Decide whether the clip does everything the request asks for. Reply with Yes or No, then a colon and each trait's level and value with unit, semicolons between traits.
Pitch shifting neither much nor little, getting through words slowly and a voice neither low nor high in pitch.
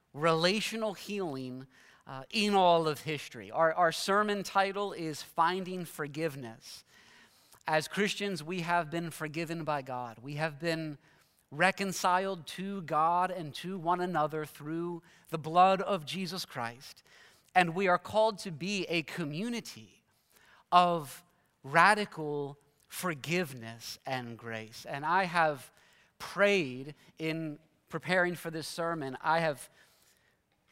Yes: average, 3.5 semitones; slow, 120 wpm; medium, 165 Hz